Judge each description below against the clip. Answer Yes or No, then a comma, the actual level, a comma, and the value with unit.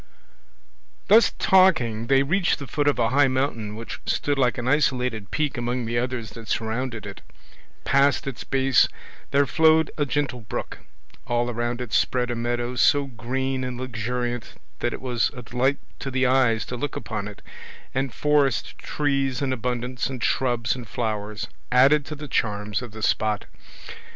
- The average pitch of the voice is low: Yes, low, 125 Hz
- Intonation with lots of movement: No, average, 2.8 semitones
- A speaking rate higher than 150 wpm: Yes, average, 170 wpm